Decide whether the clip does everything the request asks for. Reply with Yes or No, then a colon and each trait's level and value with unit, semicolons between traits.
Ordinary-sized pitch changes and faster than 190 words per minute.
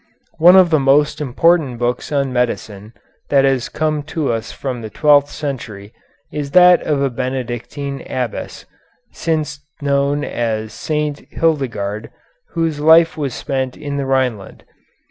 No: average, 3.6 semitones; average, 140 wpm